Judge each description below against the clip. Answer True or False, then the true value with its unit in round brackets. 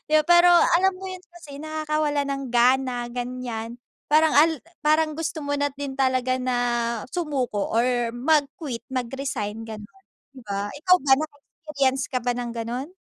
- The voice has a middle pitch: False (270 Hz)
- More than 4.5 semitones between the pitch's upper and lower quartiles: False (4.0 semitones)